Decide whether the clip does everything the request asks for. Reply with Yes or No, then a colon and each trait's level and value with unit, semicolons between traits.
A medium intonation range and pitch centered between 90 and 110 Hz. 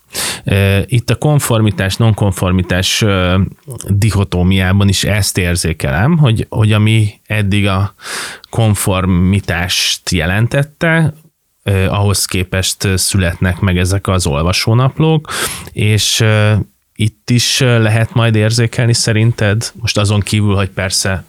Yes: average, 3.3 semitones; low, 100 Hz